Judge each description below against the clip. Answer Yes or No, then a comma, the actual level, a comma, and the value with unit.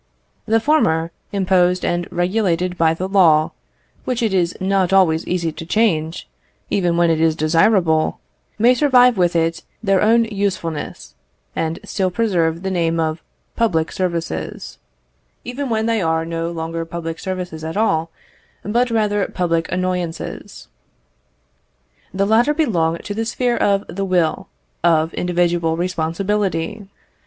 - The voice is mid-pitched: Yes, medium, 180 Hz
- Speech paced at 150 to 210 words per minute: No, slow, 135 wpm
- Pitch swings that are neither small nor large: Yes, average, 4.0 semitones